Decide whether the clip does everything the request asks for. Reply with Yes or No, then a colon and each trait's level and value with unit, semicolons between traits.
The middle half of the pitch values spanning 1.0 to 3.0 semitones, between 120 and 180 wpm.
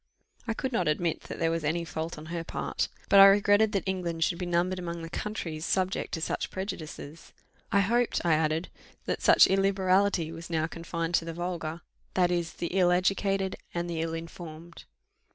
No: narrow, 2.6 semitones; average, 190 wpm